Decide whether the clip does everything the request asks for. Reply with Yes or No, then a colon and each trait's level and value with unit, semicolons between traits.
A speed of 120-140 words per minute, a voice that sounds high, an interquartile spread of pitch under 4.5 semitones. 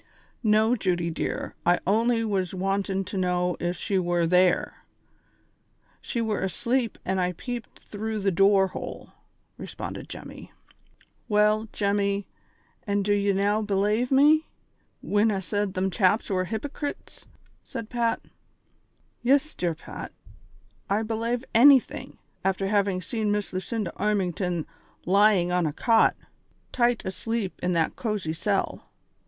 Yes: slow, 135 wpm; high, 200 Hz; average, 3.2 semitones